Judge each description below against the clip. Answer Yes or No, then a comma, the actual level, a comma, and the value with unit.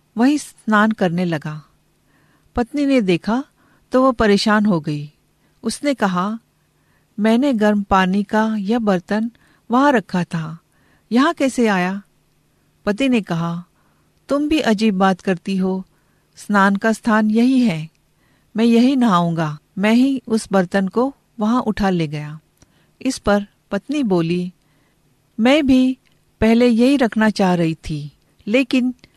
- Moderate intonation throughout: No, wide, 5.7 semitones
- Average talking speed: Yes, average, 135 wpm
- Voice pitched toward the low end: No, high, 210 Hz